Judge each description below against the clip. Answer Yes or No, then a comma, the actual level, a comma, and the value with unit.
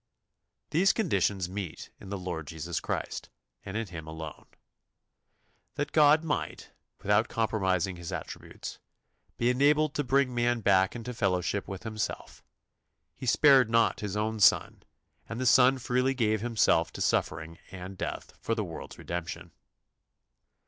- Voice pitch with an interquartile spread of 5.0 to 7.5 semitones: Yes, wide, 5.5 semitones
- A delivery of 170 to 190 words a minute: No, average, 140 wpm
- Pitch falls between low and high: No, low, 110 Hz